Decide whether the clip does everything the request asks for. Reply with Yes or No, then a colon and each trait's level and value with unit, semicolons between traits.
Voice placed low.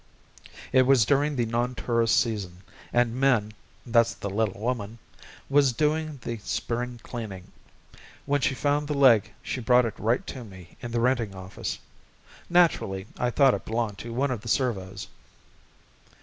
Yes: low, 120 Hz